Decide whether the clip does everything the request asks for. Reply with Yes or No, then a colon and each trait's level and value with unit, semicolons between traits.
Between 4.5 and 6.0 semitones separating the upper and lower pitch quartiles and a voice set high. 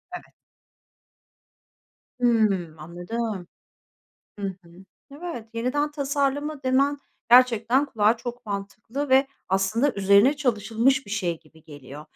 Yes: wide, 5.5 semitones; high, 230 Hz